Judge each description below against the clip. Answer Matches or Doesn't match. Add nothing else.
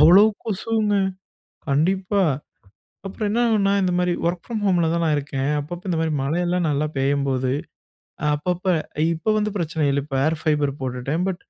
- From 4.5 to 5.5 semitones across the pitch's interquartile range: Matches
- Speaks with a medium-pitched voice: Matches